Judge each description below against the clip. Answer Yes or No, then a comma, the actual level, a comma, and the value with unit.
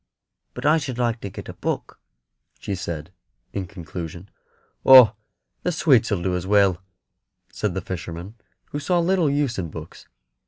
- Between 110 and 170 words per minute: Yes, average, 160 wpm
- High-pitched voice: No, low, 100 Hz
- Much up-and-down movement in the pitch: Yes, wide, 6.8 semitones